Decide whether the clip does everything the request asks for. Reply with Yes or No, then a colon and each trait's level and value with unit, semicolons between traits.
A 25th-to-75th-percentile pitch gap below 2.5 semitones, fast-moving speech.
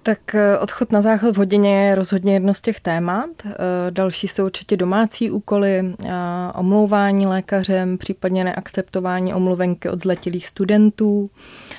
No: narrow, 2.0 semitones; average, 125 wpm